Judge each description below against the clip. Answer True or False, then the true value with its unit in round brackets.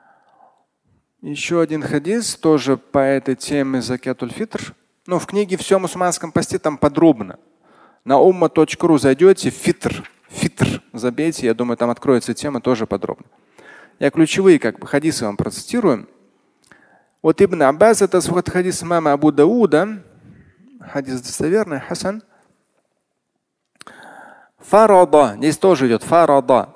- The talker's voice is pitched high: False (160 Hz)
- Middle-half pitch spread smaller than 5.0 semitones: False (5.6 semitones)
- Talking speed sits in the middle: True (120 wpm)